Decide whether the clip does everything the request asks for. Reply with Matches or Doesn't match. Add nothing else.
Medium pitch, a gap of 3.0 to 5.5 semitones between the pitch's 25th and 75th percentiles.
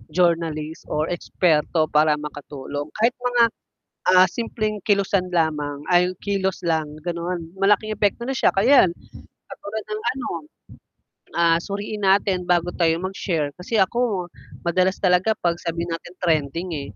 Matches